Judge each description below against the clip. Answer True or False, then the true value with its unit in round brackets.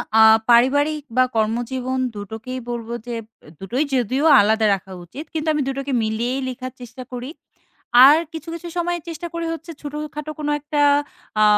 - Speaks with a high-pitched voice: True (260 Hz)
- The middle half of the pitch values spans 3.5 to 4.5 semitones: True (4.2 semitones)